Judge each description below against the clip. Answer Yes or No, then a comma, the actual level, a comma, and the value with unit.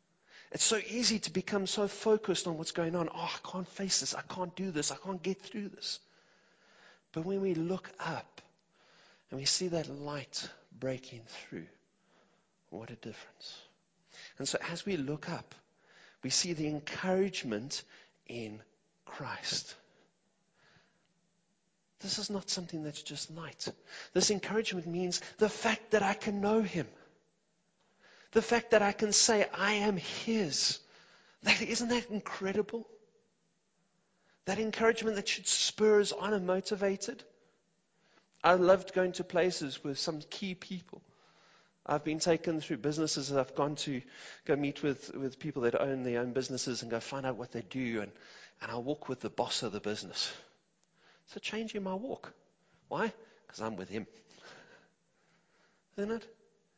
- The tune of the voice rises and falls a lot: Yes, wide, 5.8 semitones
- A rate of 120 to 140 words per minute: No, average, 155 wpm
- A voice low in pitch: No, medium, 185 Hz